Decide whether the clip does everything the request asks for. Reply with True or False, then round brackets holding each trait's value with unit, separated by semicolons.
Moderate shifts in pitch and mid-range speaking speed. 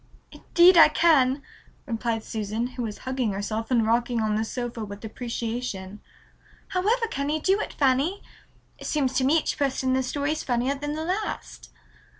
True (4.9 semitones; 175 wpm)